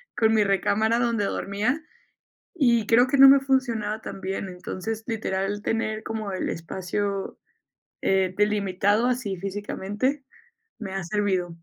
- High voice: Yes, high, 210 Hz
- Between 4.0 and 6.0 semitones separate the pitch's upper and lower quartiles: No, average, 3.0 semitones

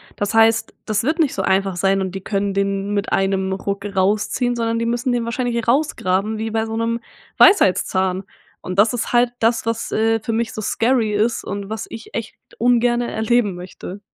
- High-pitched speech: Yes, high, 220 Hz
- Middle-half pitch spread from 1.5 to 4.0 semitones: Yes, average, 2.9 semitones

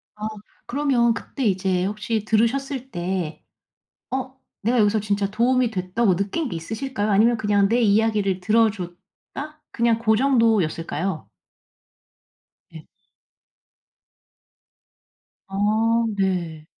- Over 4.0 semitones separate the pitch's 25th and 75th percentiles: No, average, 3.7 semitones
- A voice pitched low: No, high, 215 Hz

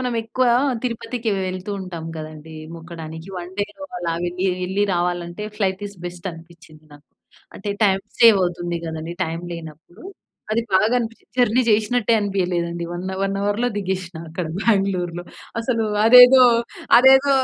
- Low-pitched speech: No, medium, 185 Hz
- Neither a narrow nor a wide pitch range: Yes, average, 4.3 semitones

